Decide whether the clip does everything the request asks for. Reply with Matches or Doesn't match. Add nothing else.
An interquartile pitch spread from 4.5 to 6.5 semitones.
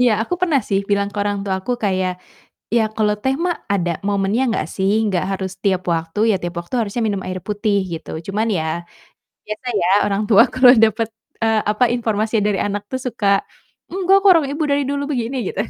Doesn't match